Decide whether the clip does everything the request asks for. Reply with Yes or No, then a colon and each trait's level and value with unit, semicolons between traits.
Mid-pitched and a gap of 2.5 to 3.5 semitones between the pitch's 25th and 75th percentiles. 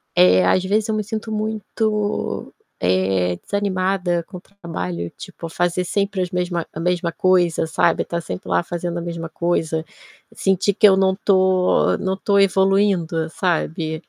Yes: medium, 180 Hz; average, 3.2 semitones